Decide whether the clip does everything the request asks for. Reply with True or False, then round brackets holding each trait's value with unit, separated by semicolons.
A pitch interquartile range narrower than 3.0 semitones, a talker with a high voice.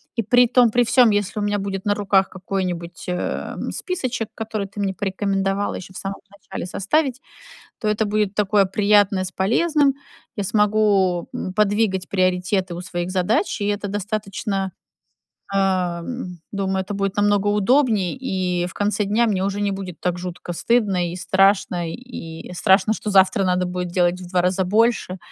True (2.4 semitones; 195 Hz)